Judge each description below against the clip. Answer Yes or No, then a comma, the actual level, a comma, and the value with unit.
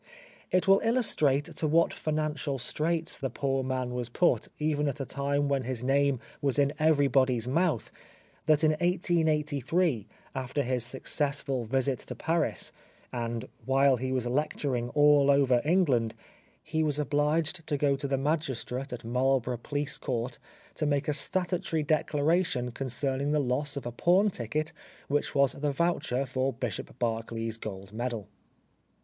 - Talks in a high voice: No, medium, 140 Hz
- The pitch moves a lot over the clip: No, average, 3.3 semitones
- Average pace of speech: Yes, average, 155 wpm